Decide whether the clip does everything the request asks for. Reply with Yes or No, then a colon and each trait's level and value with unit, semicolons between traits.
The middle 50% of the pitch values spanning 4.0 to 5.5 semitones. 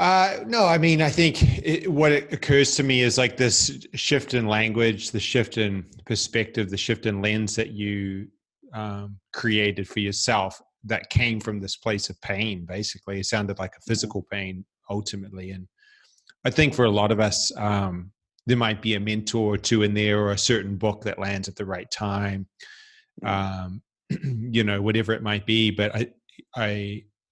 No: narrow, 2.6 semitones